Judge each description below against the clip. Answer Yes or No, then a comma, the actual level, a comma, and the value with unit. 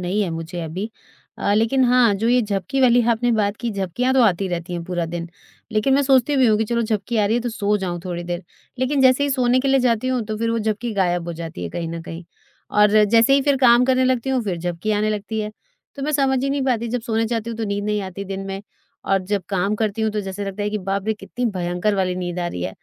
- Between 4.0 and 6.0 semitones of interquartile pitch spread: Yes, average, 4.3 semitones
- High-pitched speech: Yes, high, 215 Hz